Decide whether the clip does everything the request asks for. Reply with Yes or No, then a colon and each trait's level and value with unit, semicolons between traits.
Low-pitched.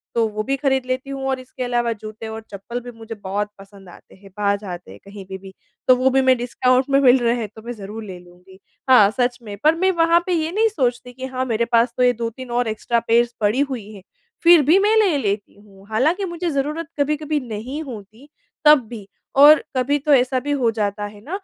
No: high, 245 Hz